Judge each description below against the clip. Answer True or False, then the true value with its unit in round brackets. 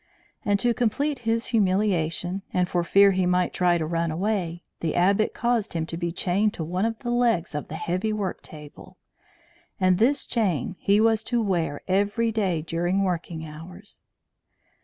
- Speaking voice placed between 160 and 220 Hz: True (185 Hz)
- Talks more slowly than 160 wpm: False (175 wpm)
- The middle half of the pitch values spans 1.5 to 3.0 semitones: False (4.1 semitones)